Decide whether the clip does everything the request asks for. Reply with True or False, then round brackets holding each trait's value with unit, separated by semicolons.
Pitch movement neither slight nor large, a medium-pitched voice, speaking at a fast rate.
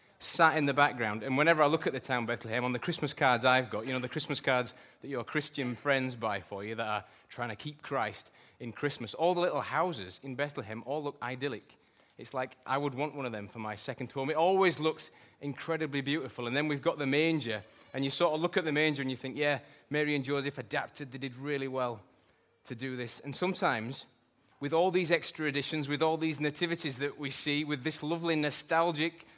True (3.3 semitones; 145 Hz; 225 wpm)